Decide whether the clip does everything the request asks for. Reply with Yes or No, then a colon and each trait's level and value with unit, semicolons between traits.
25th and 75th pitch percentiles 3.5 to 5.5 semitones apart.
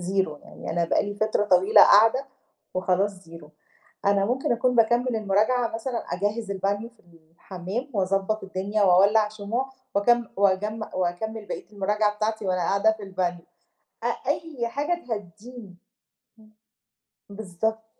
No: average, 2.9 semitones